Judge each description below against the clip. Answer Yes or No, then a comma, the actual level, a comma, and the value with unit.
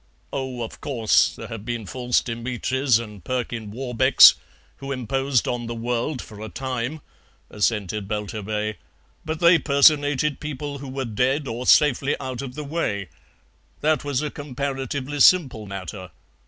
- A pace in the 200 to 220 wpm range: No, average, 145 wpm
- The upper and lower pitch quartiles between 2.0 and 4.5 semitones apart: Yes, average, 3.8 semitones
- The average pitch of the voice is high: No, low, 125 Hz